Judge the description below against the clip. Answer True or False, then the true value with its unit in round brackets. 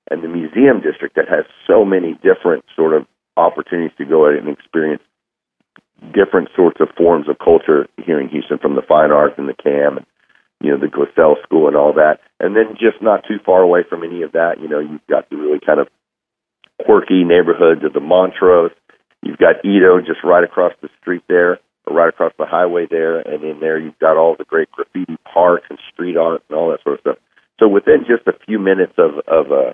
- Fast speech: True (220 wpm)